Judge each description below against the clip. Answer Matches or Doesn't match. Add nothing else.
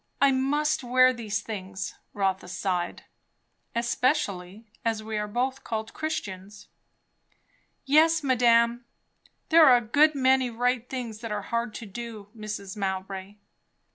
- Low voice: Doesn't match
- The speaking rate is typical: Doesn't match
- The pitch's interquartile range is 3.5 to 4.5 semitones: Matches